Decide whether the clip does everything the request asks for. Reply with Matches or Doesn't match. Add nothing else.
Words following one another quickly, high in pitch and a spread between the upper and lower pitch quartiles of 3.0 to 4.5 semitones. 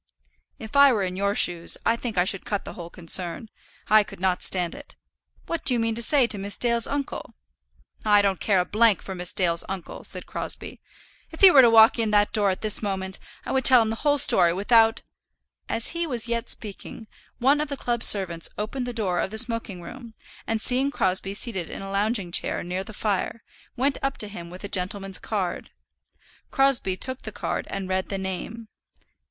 Matches